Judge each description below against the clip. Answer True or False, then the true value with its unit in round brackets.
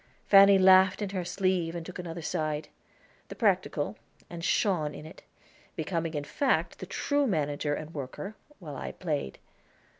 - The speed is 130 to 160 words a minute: True (155 wpm)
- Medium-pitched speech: True (170 Hz)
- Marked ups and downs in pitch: False (3.7 semitones)